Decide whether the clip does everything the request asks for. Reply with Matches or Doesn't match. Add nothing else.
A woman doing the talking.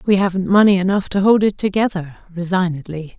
Matches